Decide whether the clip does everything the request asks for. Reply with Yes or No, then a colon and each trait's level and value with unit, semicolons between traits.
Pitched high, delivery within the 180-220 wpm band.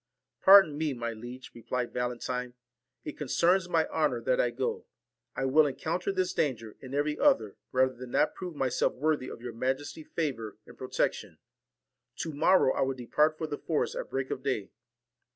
No: low, 135 Hz; average, 190 wpm